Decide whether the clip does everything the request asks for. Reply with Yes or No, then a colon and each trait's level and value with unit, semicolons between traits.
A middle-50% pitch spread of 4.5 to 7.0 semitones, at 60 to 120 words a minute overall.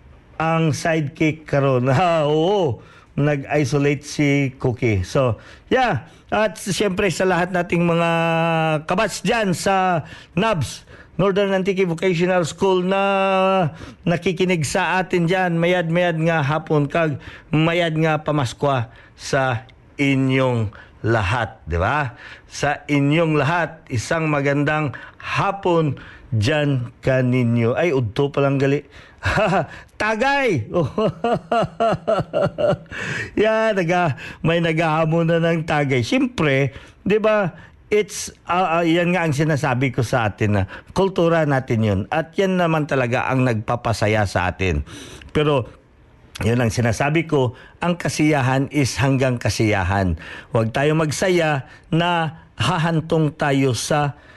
Yes: average, 5.1 semitones; average, 115 wpm